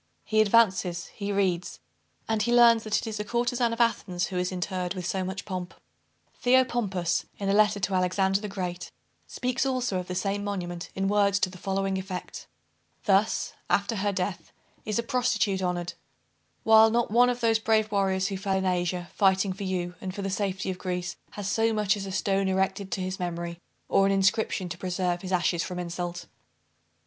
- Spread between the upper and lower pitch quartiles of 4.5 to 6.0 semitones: No, average, 2.7 semitones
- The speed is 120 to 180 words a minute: No, average, 195 wpm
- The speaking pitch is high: Yes, high, 195 Hz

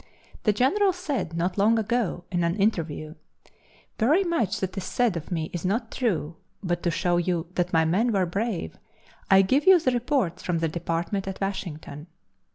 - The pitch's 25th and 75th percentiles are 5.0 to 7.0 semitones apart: Yes, wide, 5.5 semitones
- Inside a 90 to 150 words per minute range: No, average, 180 wpm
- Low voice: No, high, 190 Hz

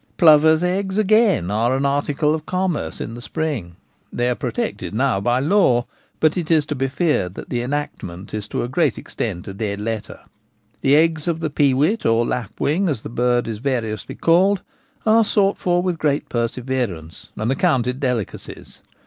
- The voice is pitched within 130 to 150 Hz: Yes, medium, 140 Hz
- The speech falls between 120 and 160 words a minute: No, average, 175 wpm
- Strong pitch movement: Yes, wide, 6.1 semitones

